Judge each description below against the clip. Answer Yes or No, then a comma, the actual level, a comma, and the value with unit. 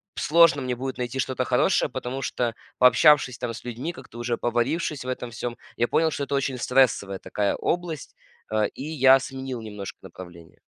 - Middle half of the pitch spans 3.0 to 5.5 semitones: No, narrow, 2.5 semitones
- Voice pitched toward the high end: No, low, 125 Hz